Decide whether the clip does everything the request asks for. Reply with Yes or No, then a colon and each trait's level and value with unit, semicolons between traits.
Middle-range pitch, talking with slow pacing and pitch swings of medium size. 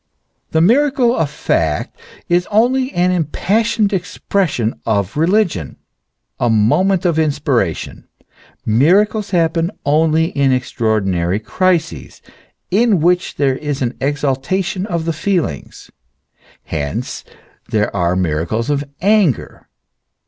No: medium, 160 Hz; slow, 110 wpm; wide, 8.3 semitones